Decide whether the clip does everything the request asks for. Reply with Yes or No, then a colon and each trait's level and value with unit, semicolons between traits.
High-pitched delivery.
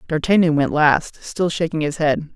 No: medium, 155 Hz